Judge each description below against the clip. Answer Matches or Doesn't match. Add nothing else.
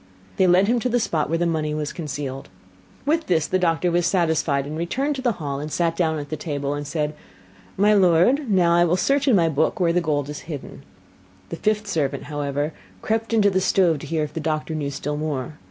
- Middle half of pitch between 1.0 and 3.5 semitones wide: Doesn't match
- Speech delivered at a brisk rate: Matches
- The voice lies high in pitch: Doesn't match